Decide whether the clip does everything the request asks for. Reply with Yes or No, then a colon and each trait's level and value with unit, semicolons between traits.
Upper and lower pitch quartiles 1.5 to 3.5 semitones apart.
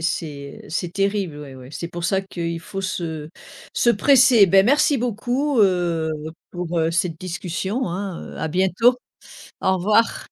No: average, 4.0 semitones